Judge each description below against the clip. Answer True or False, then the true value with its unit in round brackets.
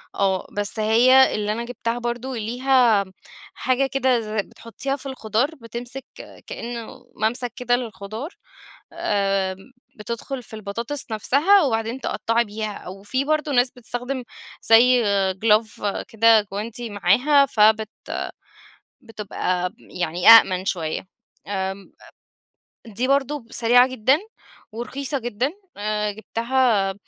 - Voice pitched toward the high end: True (230 Hz)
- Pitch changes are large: False (3.4 semitones)